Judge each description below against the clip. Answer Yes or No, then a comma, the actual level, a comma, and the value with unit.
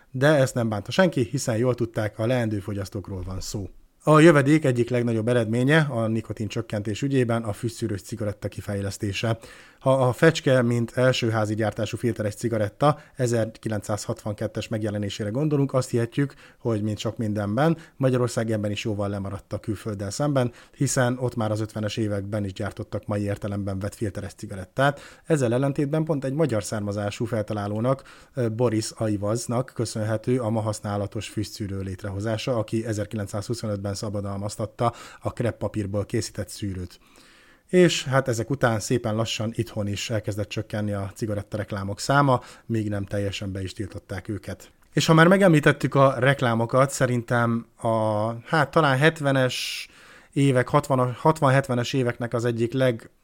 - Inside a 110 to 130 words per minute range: No, average, 140 wpm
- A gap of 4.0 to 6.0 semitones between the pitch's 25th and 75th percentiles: No, average, 3.6 semitones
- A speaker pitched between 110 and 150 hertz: Yes, low, 115 Hz